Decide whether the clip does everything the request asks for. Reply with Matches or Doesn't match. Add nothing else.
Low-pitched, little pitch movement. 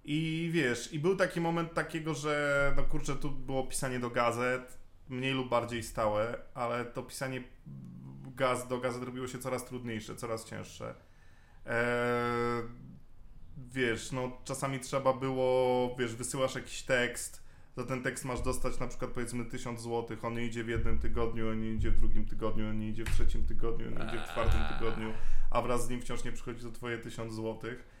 Matches